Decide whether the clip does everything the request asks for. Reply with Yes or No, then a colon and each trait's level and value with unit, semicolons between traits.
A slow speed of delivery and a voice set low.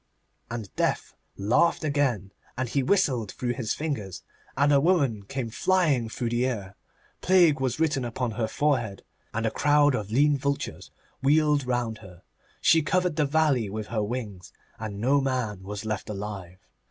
No: average, 165 wpm; low, 125 Hz